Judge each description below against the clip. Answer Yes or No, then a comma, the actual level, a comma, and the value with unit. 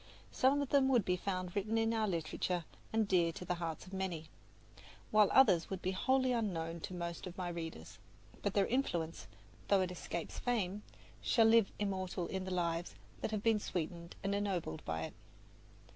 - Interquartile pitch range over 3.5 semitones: Yes, average, 3.9 semitones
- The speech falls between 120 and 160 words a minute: No, average, 185 wpm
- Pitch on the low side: No, medium, 185 Hz